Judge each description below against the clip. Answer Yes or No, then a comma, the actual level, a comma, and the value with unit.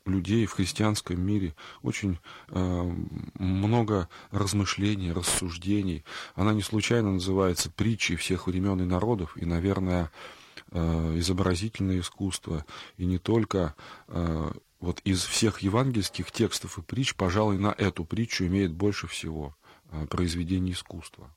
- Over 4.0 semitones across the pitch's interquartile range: No, average, 2.9 semitones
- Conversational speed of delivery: Yes, average, 125 wpm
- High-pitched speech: No, very low, 95 Hz